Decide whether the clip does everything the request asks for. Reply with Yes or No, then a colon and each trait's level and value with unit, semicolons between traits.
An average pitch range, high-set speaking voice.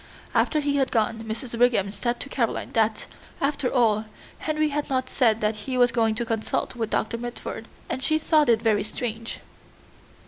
Yes: average, 3.1 semitones; high, 235 Hz